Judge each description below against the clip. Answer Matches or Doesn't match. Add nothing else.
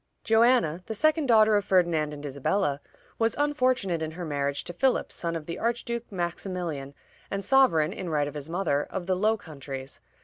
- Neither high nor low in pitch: Matches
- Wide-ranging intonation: Matches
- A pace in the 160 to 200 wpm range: Matches